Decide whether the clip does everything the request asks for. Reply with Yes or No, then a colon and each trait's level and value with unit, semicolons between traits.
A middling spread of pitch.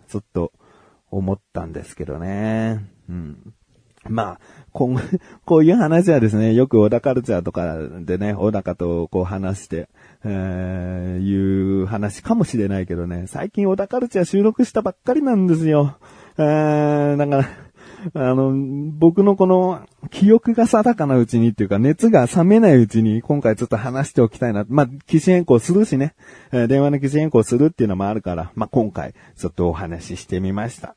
No: wide, 8.6 semitones